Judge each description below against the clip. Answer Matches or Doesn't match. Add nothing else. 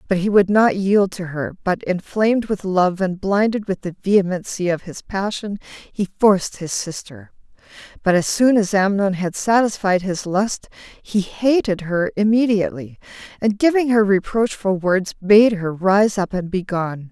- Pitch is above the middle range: Matches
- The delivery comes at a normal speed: Matches